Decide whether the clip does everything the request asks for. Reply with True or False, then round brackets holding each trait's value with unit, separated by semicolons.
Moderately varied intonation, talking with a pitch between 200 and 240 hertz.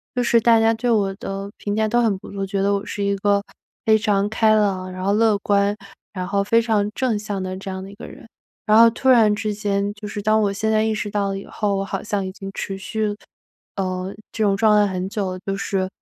False (1.7 semitones; 205 Hz)